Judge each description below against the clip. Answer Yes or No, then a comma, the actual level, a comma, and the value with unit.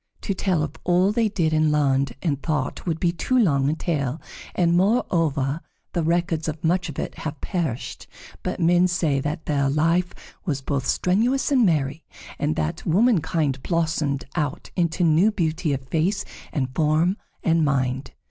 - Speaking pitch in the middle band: Yes, medium, 160 Hz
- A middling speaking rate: Yes, average, 165 wpm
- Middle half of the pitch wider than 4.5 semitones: No, average, 3.9 semitones